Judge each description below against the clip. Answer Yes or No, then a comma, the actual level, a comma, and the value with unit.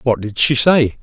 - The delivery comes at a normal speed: No, fast, 235 wpm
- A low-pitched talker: Yes, low, 125 Hz